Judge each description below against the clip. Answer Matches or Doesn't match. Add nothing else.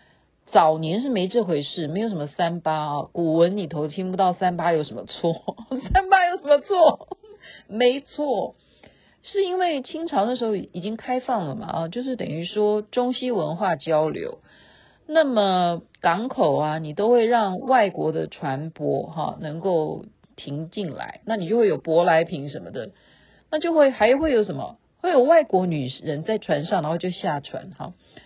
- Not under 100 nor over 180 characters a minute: Doesn't match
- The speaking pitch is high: Matches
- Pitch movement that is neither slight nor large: Doesn't match